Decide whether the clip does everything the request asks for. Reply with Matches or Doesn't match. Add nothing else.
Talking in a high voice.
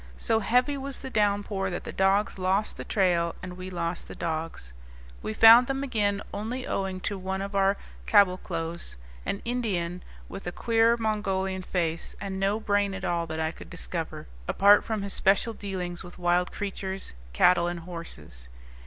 Matches